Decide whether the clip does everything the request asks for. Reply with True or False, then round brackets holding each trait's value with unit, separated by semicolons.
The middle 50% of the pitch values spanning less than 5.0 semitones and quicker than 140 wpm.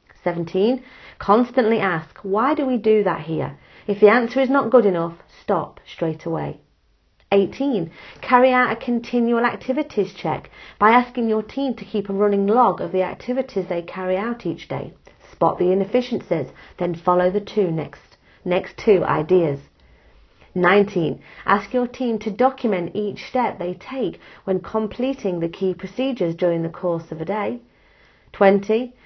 False (5.3 semitones; 155 wpm)